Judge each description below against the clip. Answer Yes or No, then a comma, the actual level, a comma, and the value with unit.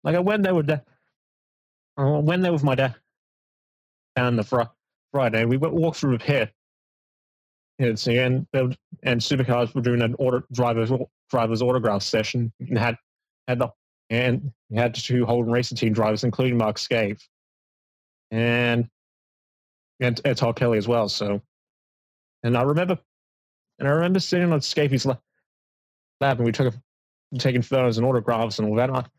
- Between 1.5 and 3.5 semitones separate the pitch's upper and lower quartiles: Yes, average, 2.7 semitones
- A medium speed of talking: Yes, average, 160 wpm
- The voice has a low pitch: Yes, low, 125 Hz